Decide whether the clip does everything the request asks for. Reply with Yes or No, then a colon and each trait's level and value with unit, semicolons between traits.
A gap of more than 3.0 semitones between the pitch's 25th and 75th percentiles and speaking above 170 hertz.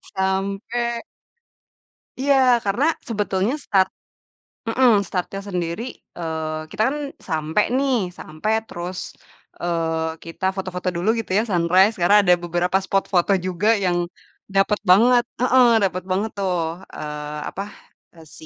Yes: average, 3.5 semitones; high, 190 Hz